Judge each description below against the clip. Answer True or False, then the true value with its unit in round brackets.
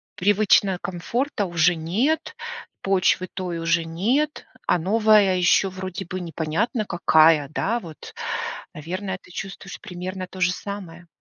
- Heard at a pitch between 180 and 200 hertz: True (185 Hz)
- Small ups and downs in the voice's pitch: False (3.1 semitones)